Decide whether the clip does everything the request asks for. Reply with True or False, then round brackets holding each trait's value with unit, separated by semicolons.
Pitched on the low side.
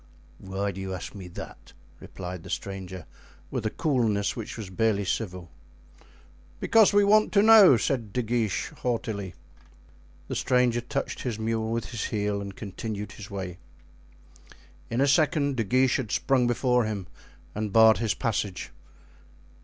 True (110 Hz)